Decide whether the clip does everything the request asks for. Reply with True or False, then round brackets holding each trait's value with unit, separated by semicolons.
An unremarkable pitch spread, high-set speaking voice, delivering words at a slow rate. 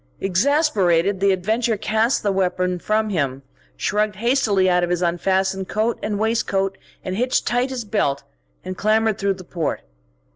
False (3.2 semitones; 200 Hz; 150 wpm)